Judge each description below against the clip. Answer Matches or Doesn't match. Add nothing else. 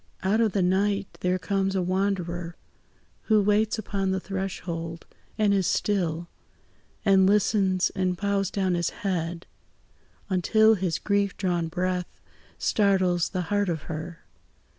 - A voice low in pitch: Doesn't match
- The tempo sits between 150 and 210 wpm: Doesn't match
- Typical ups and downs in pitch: Doesn't match